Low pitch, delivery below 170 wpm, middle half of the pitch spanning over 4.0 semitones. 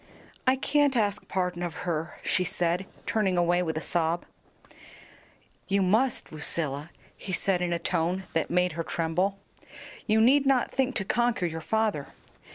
No: medium, 180 Hz; average, 160 wpm; average, 4.6 semitones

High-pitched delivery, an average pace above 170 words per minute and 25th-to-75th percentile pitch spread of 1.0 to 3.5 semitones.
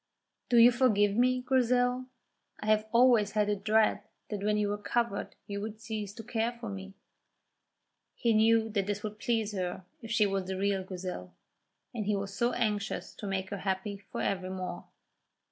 Yes: high, 210 Hz; average, 180 wpm; narrow, 2.6 semitones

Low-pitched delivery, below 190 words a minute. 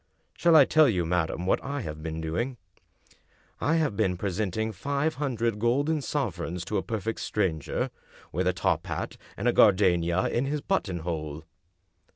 Yes: low, 105 Hz; average, 160 wpm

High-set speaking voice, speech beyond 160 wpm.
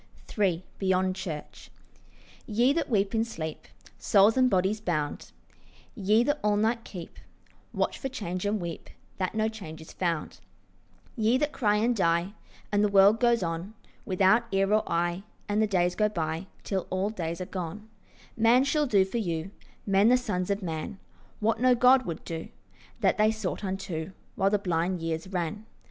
Yes: high, 195 Hz; average, 175 wpm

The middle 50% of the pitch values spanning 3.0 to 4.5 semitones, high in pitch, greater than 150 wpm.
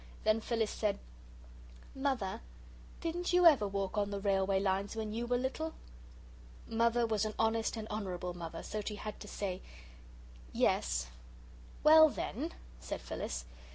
No: average, 3.5 semitones; high, 215 Hz; average, 145 wpm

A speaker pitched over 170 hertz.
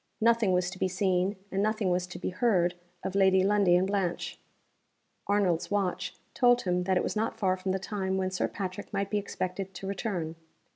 Yes: high, 190 Hz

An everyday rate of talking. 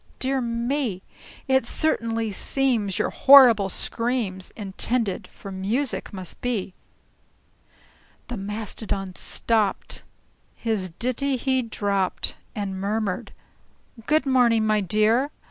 No: slow, 100 wpm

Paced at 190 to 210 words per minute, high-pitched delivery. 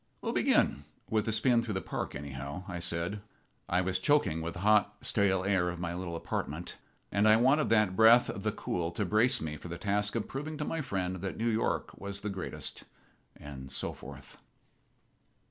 No: average, 195 wpm; very low, 95 Hz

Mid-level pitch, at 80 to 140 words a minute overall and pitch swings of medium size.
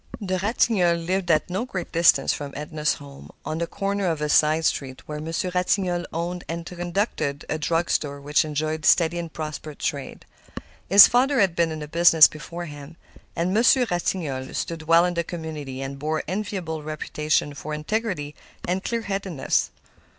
No: medium, 165 Hz; average, 175 wpm; average, 3.1 semitones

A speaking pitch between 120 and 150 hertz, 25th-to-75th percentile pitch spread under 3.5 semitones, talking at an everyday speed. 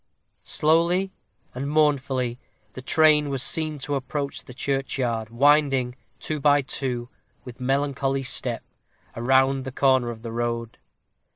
No: low, 135 Hz; average, 2.7 semitones; slow, 125 wpm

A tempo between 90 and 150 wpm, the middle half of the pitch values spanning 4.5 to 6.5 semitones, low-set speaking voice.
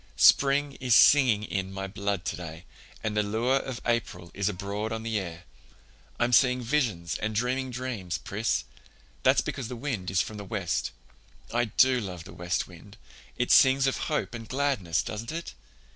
No: average, 175 wpm; average, 4.8 semitones; low, 110 Hz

